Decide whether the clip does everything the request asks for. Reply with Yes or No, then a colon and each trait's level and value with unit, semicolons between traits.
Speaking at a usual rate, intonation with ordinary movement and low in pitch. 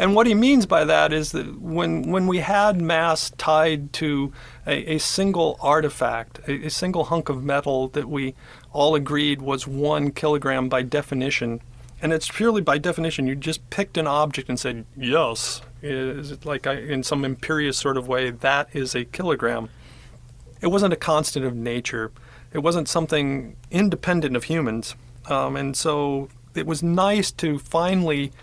No: average, 170 wpm; average, 3.9 semitones; medium, 145 Hz